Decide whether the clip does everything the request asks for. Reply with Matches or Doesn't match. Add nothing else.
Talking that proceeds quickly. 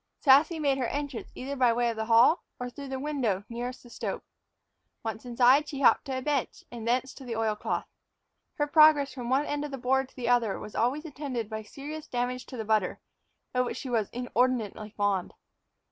Matches